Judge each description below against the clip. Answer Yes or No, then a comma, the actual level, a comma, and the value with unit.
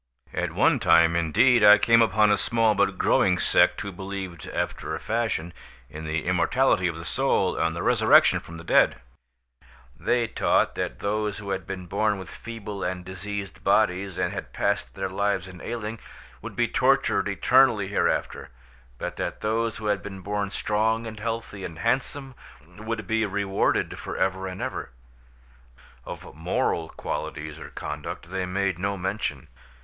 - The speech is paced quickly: No, average, 165 wpm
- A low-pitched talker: Yes, low, 100 Hz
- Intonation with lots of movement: No, average, 3.2 semitones